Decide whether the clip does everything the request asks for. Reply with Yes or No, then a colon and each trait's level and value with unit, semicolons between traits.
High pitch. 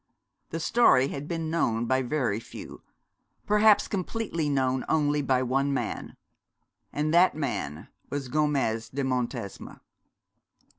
No: medium, 140 Hz